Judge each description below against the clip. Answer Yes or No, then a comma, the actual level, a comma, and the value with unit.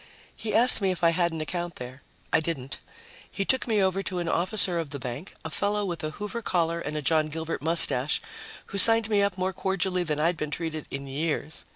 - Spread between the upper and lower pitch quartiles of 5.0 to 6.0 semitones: No, average, 3.9 semitones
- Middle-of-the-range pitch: Yes, medium, 170 Hz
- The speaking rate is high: Yes, fast, 225 wpm